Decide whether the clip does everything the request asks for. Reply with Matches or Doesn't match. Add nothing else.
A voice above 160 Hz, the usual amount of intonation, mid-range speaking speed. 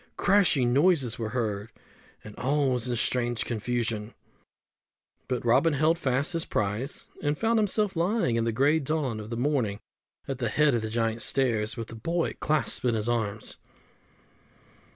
Doesn't match